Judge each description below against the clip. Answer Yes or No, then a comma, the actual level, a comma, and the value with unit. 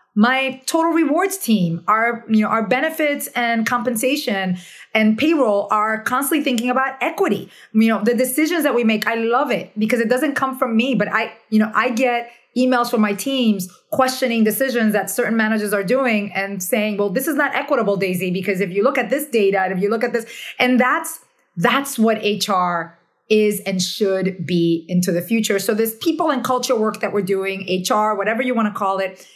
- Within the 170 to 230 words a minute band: Yes, fast, 205 wpm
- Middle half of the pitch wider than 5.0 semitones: No, average, 4.0 semitones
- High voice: Yes, high, 225 Hz